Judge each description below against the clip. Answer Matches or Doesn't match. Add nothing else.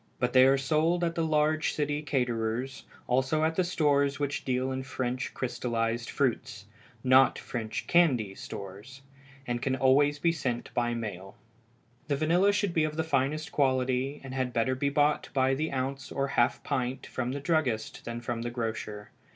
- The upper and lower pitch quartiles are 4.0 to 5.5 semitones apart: Doesn't match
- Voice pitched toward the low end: Matches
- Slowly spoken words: Doesn't match